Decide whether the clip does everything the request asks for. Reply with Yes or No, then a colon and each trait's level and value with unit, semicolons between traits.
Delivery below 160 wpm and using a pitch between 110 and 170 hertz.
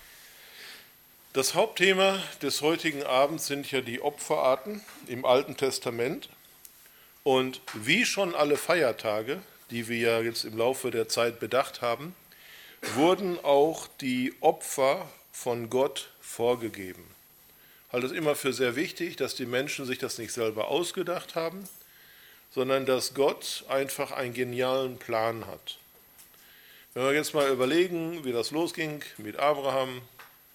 Yes: average, 135 wpm; low, 135 Hz